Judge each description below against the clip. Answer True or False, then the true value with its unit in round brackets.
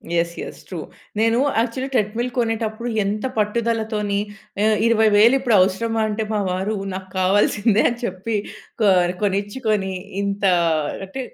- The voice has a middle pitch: False (215 Hz)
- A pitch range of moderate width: False (2.3 semitones)